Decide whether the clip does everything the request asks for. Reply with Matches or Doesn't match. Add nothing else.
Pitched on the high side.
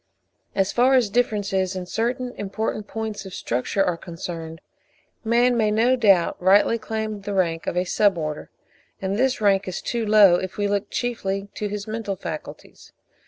Matches